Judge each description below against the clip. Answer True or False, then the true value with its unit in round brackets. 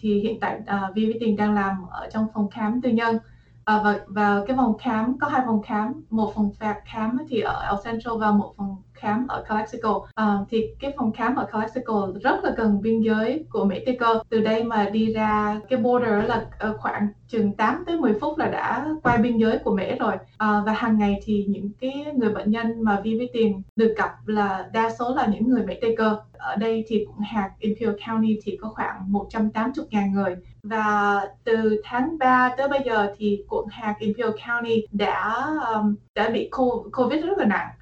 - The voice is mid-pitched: False (220 Hz)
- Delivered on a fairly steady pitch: True (1.9 semitones)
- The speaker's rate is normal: True (210 wpm)